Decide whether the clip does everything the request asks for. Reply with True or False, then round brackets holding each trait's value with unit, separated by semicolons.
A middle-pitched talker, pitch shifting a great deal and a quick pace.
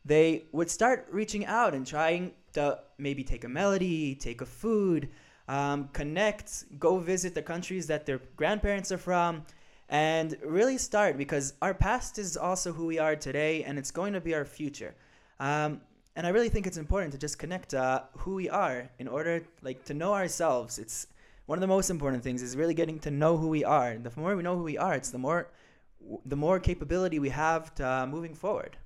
False (155 Hz; 4.6 semitones; 210 wpm)